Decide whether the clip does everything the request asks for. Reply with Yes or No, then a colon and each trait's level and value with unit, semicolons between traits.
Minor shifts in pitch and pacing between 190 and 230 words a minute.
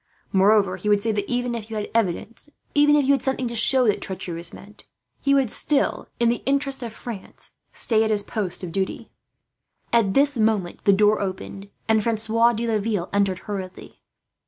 No: average, 3.2 semitones; average, 195 wpm